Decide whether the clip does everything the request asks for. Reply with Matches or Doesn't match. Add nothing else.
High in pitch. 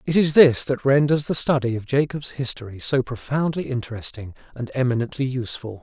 Doesn't match